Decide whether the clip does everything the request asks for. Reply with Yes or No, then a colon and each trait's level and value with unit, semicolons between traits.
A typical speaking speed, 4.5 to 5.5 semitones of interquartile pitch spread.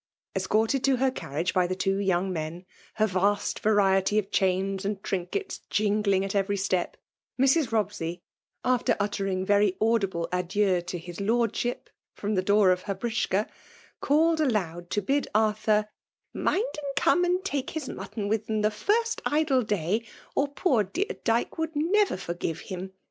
Yes: average, 170 wpm; average, 5.2 semitones